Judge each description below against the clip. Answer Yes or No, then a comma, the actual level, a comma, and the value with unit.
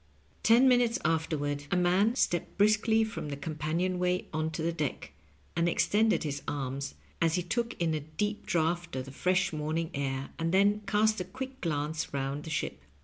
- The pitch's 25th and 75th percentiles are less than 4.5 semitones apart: No, wide, 5.4 semitones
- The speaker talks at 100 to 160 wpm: No, average, 185 wpm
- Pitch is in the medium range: Yes, medium, 165 Hz